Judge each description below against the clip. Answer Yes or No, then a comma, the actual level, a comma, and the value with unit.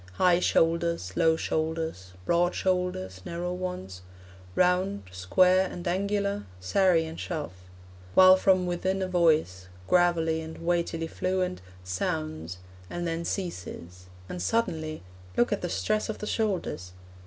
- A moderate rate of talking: No, slow, 130 wpm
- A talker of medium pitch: Yes, medium, 170 Hz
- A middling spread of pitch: Yes, average, 3.1 semitones